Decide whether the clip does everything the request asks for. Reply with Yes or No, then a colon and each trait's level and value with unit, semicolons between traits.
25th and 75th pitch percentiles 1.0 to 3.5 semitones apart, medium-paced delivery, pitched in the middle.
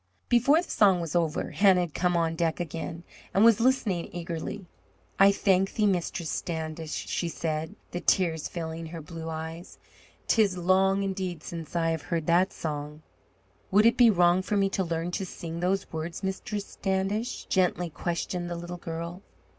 Yes: average, 2.8 semitones; average, 170 wpm; medium, 175 Hz